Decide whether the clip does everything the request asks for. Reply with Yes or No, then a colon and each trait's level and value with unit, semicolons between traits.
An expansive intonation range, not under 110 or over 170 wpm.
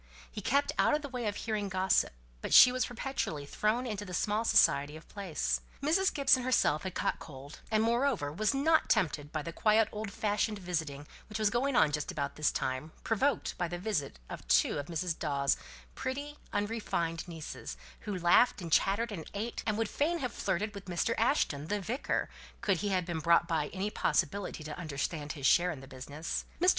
No: wide, 6.4 semitones; average, 200 wpm